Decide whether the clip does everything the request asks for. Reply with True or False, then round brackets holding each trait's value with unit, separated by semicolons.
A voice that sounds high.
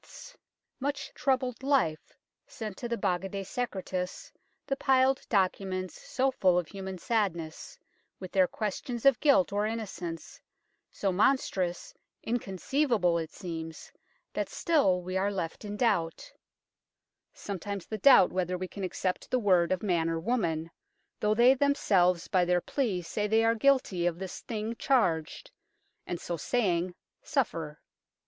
True (195 Hz)